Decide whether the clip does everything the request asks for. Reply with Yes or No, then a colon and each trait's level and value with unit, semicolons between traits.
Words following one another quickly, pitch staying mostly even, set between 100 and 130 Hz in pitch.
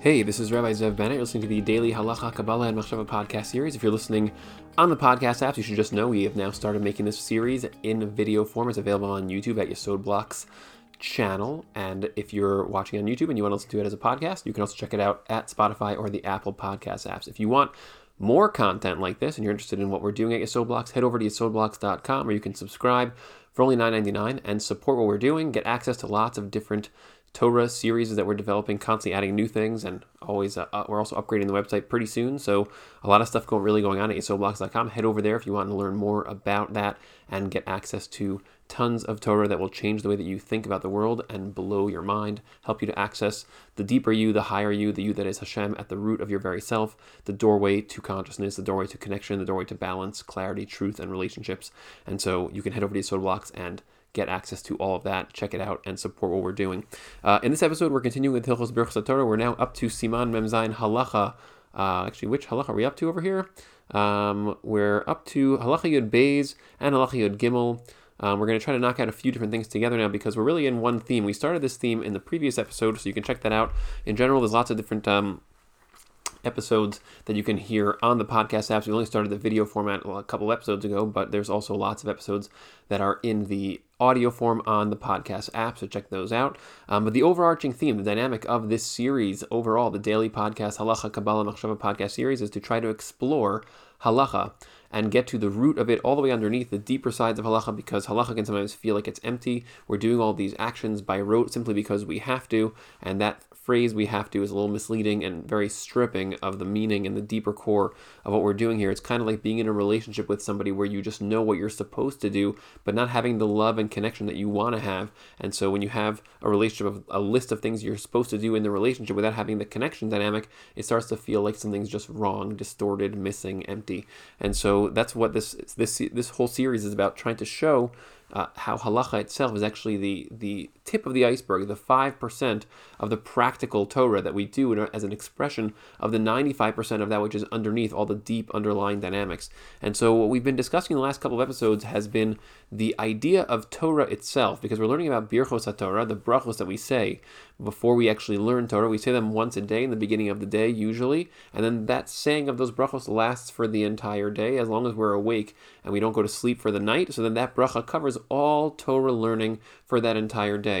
Yes: fast, 240 wpm; narrow, 2.3 semitones; low, 110 Hz